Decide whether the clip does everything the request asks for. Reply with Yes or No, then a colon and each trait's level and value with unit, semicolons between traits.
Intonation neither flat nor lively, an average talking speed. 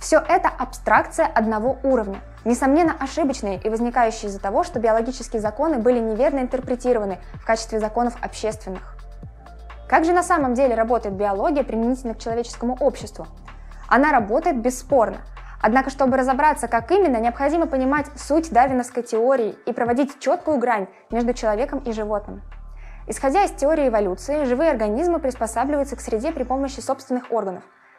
Yes: average, 3.7 semitones; average, 140 wpm